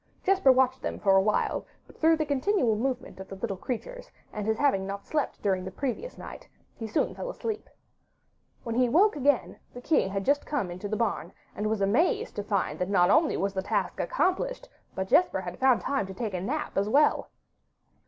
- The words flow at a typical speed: No, fast, 215 wpm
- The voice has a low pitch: No, high, 240 Hz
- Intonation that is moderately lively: No, wide, 7.3 semitones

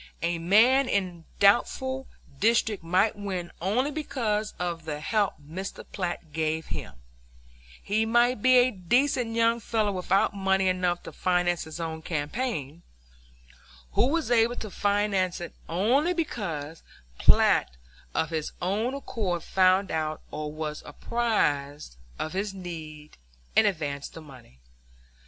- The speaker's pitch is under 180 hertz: No, high, 190 Hz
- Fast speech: No, slow, 135 wpm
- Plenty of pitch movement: Yes, wide, 5.8 semitones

